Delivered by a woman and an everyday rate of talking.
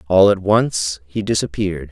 No: male; average, 155 wpm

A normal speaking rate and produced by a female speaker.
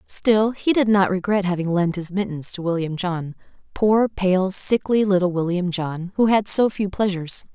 Yes: average, 175 wpm; female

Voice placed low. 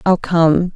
No: medium, 170 Hz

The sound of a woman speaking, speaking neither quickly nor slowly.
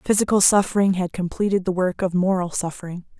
Yes: female; average, 170 wpm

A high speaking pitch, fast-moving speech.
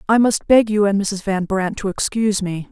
Yes: high, 205 Hz; fast, 245 wpm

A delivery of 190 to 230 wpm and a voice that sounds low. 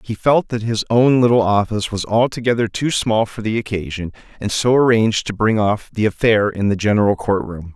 Yes: average, 200 wpm; low, 110 Hz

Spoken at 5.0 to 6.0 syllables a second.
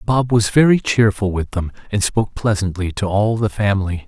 Yes: 5.3 syllables/s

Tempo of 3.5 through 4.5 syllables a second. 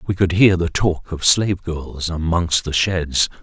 Yes: 4.1 syllables/s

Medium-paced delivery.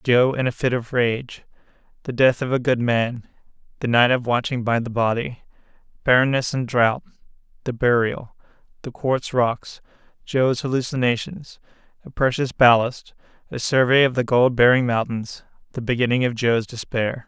No: slow, 120 wpm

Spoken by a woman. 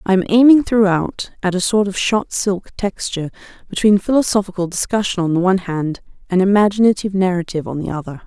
Yes: female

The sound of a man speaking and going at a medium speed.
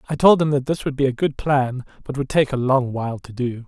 No: male; fast, 295 wpm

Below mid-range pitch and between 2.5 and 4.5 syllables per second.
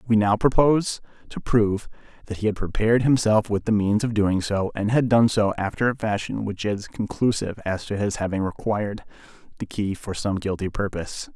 No: low, 105 Hz; 5.5 syllables/s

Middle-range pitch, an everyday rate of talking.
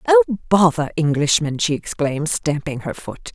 Yes: medium, 160 Hz; average, 145 wpm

